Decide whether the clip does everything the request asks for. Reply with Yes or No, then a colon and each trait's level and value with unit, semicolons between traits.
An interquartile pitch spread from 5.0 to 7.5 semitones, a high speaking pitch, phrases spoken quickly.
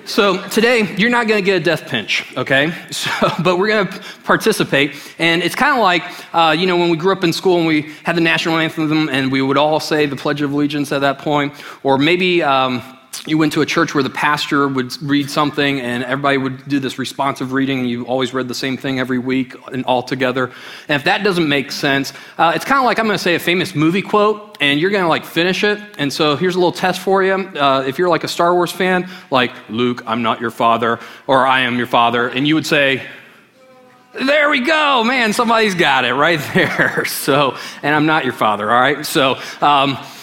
No: average, 5.3 semitones; medium, 155 Hz; fast, 235 wpm